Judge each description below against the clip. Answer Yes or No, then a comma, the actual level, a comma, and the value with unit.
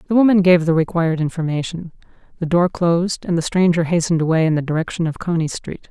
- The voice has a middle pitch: Yes, medium, 170 Hz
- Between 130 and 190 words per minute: No, fast, 205 wpm